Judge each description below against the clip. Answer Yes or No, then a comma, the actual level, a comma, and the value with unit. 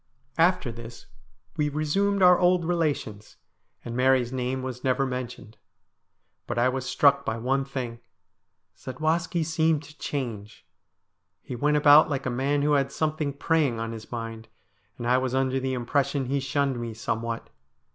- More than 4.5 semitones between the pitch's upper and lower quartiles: No, average, 3.7 semitones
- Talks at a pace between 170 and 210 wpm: No, average, 155 wpm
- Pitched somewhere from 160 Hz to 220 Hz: No, low, 135 Hz